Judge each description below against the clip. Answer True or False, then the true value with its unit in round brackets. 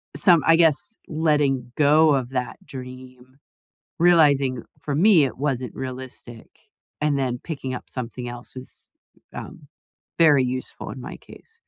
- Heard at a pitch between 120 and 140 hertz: True (135 Hz)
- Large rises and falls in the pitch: False (3.1 semitones)